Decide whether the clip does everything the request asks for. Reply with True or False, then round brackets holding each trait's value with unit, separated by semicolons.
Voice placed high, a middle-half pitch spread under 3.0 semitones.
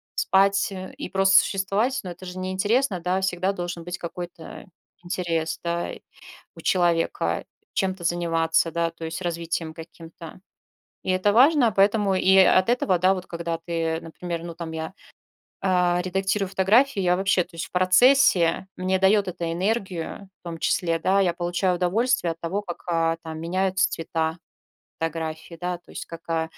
False (180 Hz; 2.4 semitones)